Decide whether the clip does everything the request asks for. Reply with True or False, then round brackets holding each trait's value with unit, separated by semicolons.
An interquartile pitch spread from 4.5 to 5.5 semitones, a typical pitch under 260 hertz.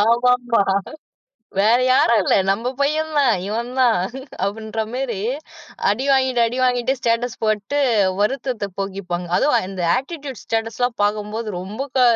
False (3.4 semitones; 230 Hz)